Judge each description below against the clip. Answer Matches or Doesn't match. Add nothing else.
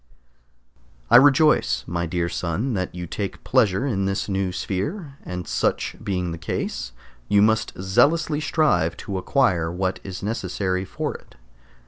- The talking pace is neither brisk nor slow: Matches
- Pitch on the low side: Matches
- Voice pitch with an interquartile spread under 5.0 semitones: Doesn't match